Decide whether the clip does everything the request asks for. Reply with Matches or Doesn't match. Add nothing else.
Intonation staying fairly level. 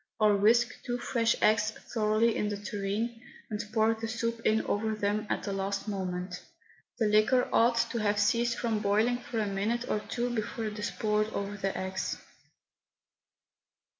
Matches